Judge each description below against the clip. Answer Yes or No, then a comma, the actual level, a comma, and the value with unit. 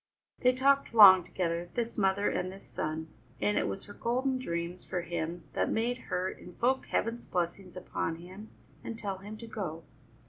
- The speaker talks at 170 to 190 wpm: Yes, average, 175 wpm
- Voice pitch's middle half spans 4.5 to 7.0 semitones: Yes, average, 5.0 semitones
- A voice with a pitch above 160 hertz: Yes, high, 190 Hz